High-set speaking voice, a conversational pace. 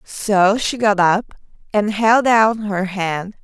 Yes: high, 205 Hz; average, 155 wpm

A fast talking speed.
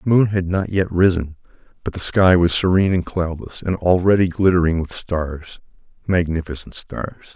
No: average, 155 wpm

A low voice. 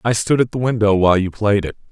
Yes: low, 105 Hz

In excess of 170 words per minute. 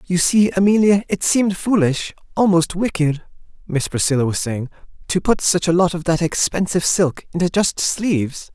No: average, 160 wpm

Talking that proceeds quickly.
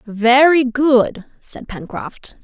No: slow, 100 wpm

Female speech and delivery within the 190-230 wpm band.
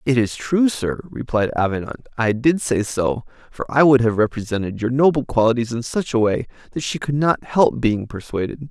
No: male; average, 200 wpm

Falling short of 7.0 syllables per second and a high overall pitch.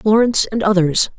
Yes: 5.7 syllables/s; high, 205 Hz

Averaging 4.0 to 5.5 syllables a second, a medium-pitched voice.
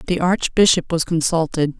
Yes: 5.0 syllables/s; medium, 165 Hz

